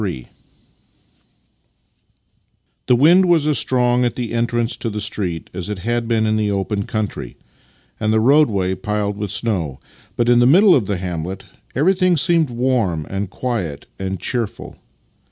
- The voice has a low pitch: Yes, low, 110 Hz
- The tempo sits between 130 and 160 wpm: Yes, average, 155 wpm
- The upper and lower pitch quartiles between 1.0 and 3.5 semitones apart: No, average, 4.2 semitones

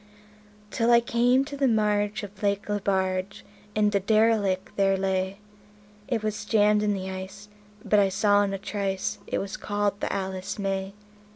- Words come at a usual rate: Yes, average, 170 wpm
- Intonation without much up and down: Yes, narrow, 1.7 semitones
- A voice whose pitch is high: Yes, high, 205 Hz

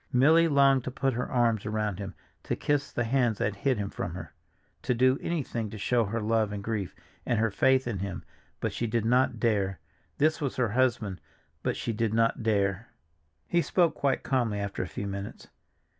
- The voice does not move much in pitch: No, average, 4.1 semitones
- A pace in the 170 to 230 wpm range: Yes, average, 200 wpm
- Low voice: Yes, low, 115 Hz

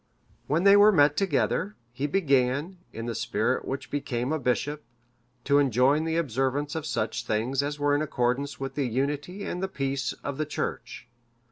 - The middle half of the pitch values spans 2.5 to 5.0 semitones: Yes, average, 2.9 semitones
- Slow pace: No, average, 175 wpm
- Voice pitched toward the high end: No, medium, 140 Hz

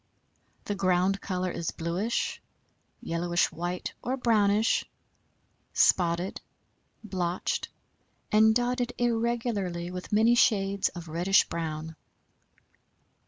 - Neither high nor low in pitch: No, high, 195 Hz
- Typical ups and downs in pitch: Yes, average, 4.2 semitones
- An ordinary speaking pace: No, slow, 90 wpm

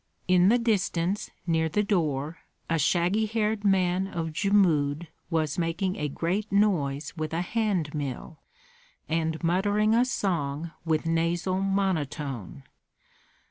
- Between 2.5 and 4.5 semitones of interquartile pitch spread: Yes, average, 4.0 semitones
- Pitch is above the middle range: No, medium, 170 Hz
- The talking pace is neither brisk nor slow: No, slow, 125 wpm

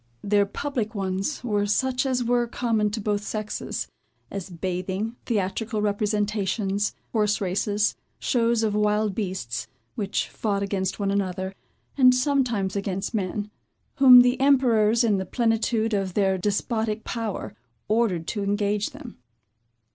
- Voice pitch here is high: Yes, high, 210 Hz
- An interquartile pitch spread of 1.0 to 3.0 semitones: Yes, average, 2.7 semitones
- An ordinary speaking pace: No, slow, 130 wpm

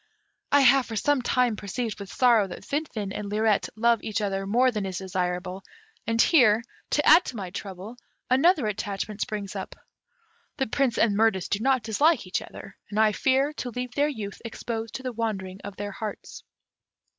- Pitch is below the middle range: No, high, 220 Hz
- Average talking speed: Yes, average, 185 wpm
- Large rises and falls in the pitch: No, average, 4.0 semitones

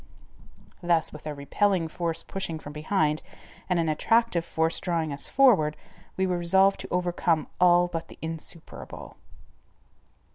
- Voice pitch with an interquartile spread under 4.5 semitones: Yes, narrow, 2.4 semitones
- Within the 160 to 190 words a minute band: No, average, 140 wpm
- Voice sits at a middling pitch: Yes, medium, 170 Hz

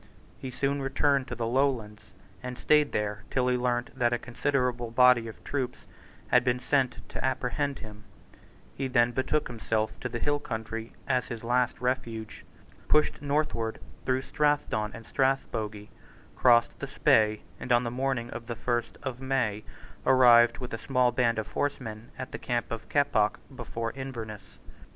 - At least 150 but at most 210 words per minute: Yes, average, 165 wpm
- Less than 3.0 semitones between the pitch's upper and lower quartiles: Yes, narrow, 2.5 semitones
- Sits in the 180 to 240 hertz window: No, low, 125 Hz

